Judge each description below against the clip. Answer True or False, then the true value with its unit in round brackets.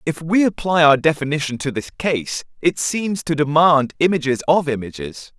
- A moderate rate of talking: True (165 wpm)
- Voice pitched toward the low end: False (150 Hz)